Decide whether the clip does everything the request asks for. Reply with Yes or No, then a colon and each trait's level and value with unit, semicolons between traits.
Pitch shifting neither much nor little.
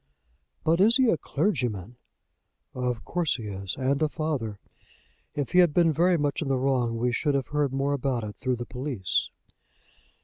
Yes: average, 4.3 semitones